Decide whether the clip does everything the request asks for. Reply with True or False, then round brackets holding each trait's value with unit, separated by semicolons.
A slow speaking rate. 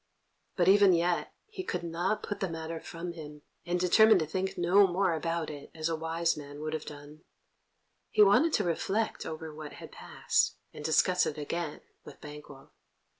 False (180 wpm)